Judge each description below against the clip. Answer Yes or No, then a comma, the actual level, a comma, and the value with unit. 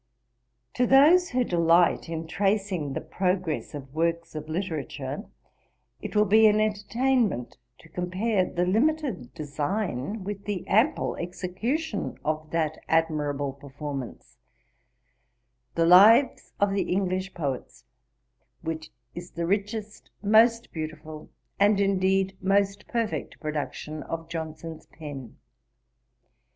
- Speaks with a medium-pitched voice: Yes, medium, 180 Hz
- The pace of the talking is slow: Yes, slow, 115 wpm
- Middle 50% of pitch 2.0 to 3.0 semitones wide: No, average, 4.9 semitones